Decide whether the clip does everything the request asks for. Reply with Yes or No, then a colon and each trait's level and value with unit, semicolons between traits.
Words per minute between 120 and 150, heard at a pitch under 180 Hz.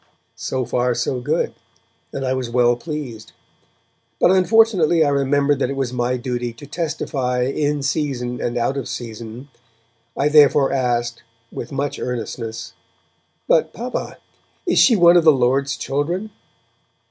Yes: average, 145 wpm; low, 135 Hz